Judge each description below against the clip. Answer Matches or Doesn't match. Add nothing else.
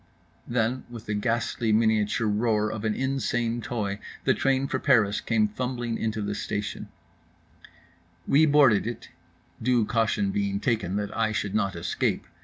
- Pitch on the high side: Doesn't match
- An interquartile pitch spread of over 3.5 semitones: Doesn't match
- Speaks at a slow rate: Doesn't match